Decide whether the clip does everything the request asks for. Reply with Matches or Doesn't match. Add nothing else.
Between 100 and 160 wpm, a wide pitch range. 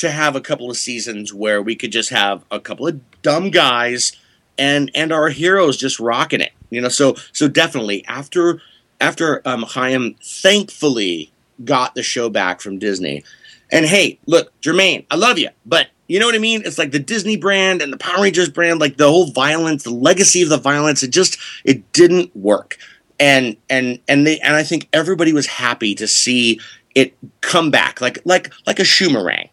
Doesn't match